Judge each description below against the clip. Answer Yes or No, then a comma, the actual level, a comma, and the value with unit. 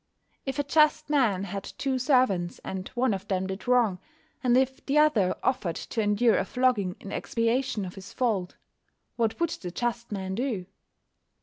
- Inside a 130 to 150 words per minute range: No, average, 175 wpm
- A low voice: No, high, 230 Hz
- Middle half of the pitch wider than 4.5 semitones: Yes, average, 5.2 semitones